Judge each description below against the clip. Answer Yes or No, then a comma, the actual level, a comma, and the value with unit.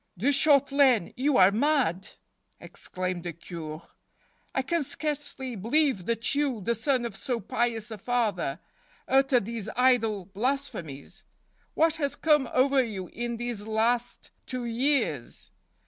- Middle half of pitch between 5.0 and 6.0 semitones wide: Yes, wide, 5.4 semitones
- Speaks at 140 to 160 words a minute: Yes, average, 145 wpm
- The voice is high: Yes, high, 240 Hz